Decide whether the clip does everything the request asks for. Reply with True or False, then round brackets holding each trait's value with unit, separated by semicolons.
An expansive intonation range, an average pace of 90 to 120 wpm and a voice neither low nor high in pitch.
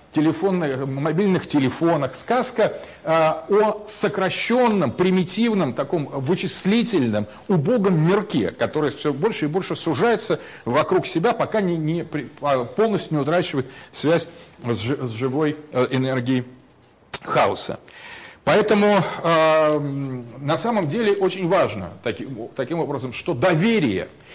True (5.8 semitones; 115 wpm; 165 Hz)